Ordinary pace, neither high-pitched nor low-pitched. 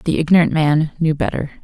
Yes: average, 185 wpm; medium, 155 Hz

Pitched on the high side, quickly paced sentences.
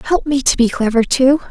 Yes: very high, 260 Hz; fast, 240 wpm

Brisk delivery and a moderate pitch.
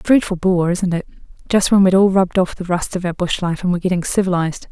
Yes: fast, 255 wpm; medium, 180 Hz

